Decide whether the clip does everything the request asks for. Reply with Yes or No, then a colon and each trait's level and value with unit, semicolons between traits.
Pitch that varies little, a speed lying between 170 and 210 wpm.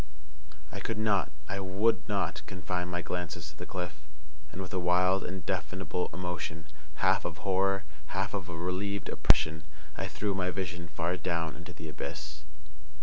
No: narrow, 2.2 semitones; average, 160 wpm